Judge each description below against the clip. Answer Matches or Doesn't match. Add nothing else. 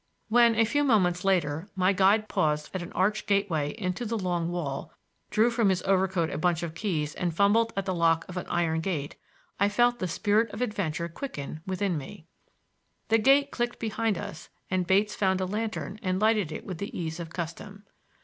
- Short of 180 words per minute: Doesn't match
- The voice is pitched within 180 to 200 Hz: Matches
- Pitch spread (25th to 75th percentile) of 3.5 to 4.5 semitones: Matches